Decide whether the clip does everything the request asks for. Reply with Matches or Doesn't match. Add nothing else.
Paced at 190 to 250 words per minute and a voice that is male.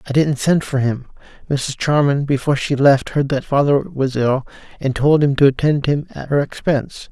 Matches